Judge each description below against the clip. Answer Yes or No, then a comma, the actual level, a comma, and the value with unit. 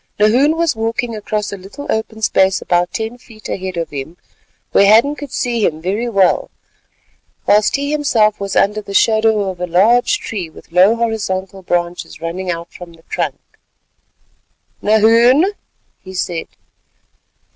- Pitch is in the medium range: No, high, 210 Hz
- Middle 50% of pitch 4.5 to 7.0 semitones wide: No, average, 3.9 semitones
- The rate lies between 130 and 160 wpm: Yes, average, 150 wpm